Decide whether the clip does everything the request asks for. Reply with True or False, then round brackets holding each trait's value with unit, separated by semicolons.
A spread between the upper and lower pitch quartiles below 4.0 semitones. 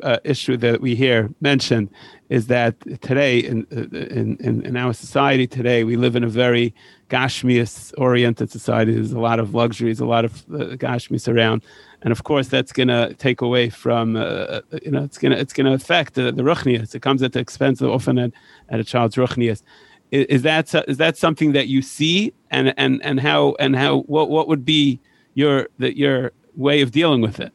True (3.0 semitones)